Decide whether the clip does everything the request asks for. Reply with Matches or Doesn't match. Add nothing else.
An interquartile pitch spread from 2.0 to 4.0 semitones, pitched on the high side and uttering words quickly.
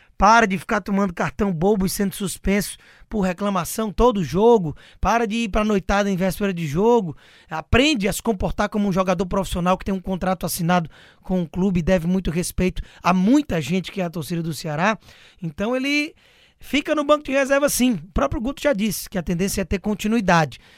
Matches